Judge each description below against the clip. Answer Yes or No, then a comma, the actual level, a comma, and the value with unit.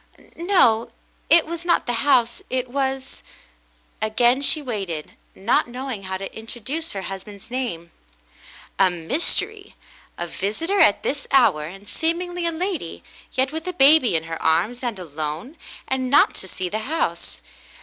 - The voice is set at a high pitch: Yes, high, 245 Hz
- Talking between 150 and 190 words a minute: Yes, average, 160 wpm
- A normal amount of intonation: No, wide, 7.7 semitones